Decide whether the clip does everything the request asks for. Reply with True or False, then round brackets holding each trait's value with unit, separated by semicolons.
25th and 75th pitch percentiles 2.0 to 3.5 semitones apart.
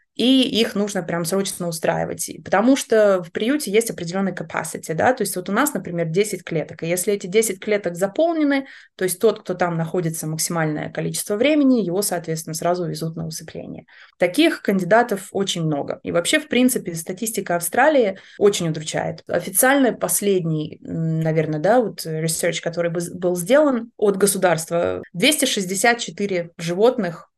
False (4.9 semitones)